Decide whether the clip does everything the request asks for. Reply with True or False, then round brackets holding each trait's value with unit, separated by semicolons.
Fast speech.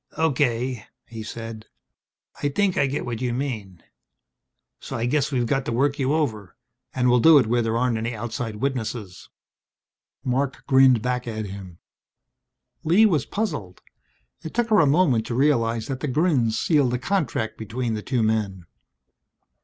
False (165 wpm)